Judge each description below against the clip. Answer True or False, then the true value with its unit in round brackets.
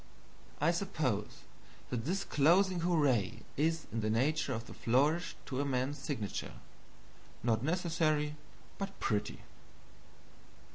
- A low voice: False (145 Hz)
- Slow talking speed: True (115 wpm)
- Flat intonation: False (5.6 semitones)